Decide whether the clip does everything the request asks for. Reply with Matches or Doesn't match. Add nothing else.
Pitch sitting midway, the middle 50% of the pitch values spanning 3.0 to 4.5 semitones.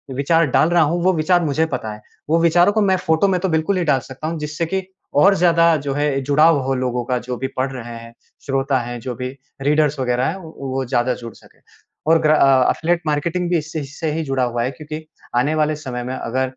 Matches